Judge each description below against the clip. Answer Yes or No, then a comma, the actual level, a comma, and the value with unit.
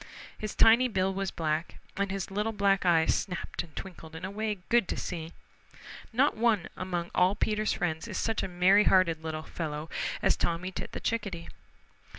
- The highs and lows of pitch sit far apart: No, average, 3.8 semitones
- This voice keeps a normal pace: Yes, average, 180 wpm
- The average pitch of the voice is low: No, medium, 185 Hz